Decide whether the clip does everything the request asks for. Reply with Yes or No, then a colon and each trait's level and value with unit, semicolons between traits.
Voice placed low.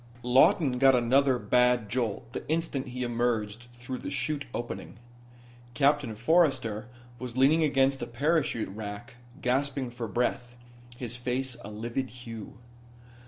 Yes: low, 125 Hz